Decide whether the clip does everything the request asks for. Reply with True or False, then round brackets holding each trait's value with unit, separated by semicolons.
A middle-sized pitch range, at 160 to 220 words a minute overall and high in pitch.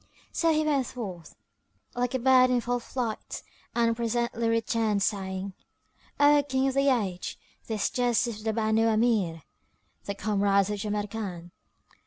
False (3.4 semitones; 150 wpm; 225 Hz)